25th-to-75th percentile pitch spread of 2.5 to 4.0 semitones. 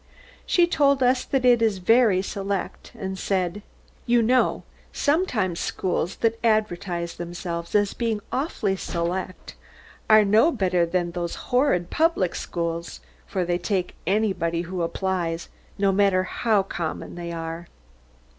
No: average, 4.5 semitones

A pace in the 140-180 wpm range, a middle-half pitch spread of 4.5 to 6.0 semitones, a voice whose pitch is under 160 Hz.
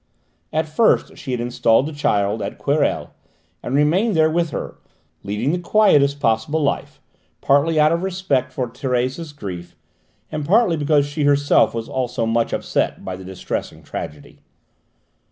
Yes: average, 155 wpm; average, 5.3 semitones; medium, 140 Hz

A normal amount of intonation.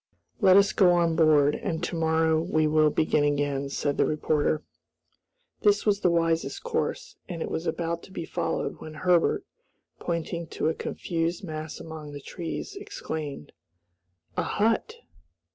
No: narrow, 2.3 semitones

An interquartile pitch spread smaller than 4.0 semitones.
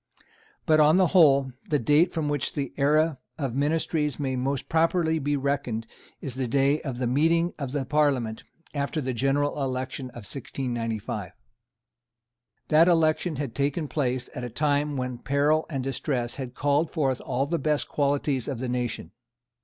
Yes: average, 3.0 semitones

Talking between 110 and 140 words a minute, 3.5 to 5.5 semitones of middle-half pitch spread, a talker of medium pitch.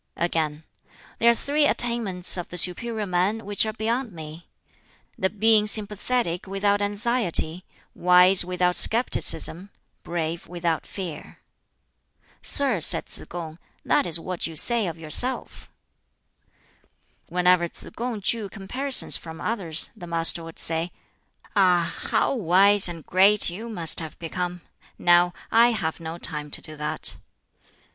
Yes: slow, 135 wpm; average, 4.3 semitones; medium, 180 Hz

